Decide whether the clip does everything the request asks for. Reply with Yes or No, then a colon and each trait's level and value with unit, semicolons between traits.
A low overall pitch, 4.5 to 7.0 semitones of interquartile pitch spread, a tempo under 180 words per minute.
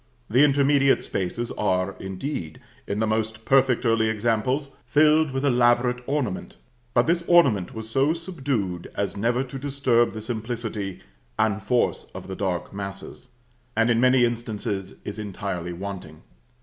Yes: low, 115 Hz; average, 4.8 semitones; average, 145 wpm